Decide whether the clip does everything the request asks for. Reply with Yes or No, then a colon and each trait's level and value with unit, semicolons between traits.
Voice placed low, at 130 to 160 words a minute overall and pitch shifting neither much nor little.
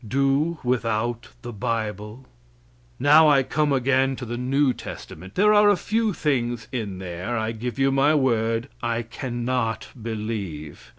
Yes: low, 120 Hz; average, 150 wpm; average, 3.5 semitones